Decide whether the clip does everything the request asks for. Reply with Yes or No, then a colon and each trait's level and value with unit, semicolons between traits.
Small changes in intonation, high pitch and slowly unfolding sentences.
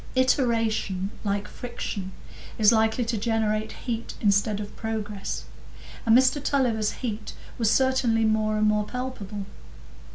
Yes: narrow, 2.3 semitones; high, 220 Hz; slow, 125 wpm